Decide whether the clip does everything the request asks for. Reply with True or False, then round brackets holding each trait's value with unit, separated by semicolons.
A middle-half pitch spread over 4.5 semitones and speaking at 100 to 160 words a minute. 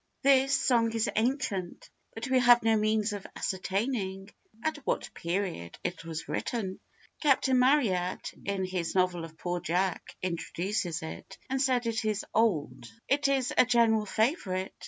True (5.2 semitones; 150 wpm)